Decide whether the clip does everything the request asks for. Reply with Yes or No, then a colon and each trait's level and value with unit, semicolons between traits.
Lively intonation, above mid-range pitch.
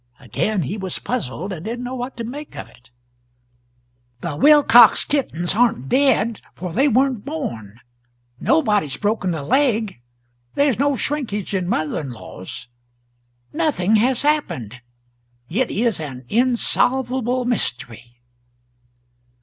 Yes: wide, 8.4 semitones; high, 220 Hz